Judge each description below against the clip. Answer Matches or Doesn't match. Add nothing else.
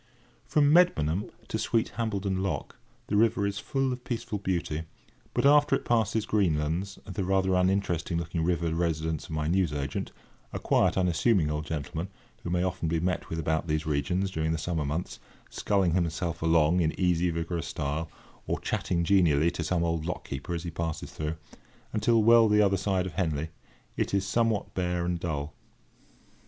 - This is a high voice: Doesn't match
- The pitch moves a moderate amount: Matches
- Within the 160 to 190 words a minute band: Matches